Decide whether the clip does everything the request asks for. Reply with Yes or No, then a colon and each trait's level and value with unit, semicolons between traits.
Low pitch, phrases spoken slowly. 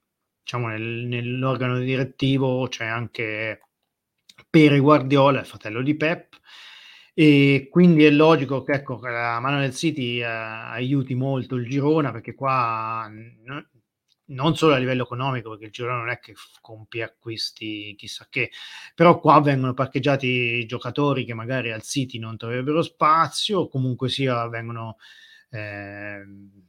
No: low, 125 Hz; average, 145 wpm